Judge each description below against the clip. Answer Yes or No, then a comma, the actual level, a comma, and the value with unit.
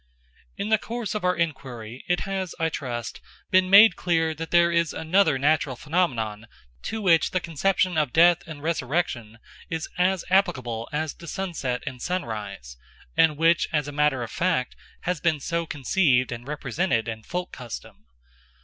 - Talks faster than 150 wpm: Yes, average, 165 wpm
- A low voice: No, medium, 160 Hz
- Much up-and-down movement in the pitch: Yes, wide, 5.9 semitones